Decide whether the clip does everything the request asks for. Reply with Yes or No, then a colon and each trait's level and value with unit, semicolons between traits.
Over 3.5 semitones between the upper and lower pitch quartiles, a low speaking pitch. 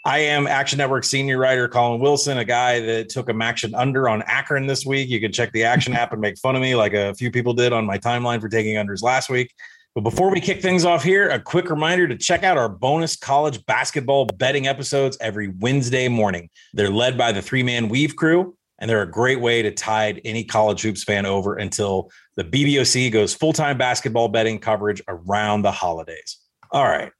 Yes: average, 4.0 semitones; low, 125 Hz